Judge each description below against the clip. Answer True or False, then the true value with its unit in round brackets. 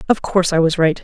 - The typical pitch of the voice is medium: True (175 Hz)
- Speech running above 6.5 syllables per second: True (7.1 syllables/s)